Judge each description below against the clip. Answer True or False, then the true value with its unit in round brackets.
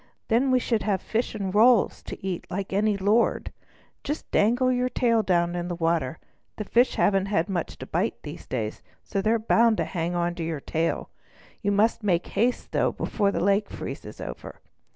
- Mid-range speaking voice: False (200 Hz)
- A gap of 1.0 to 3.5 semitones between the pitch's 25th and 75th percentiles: False (4.7 semitones)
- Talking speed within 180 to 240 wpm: True (190 wpm)